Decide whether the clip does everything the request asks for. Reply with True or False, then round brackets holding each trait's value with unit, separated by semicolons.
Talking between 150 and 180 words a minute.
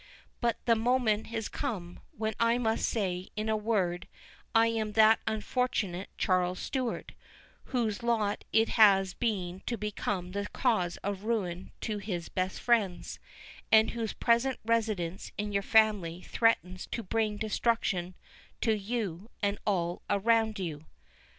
False (140 wpm)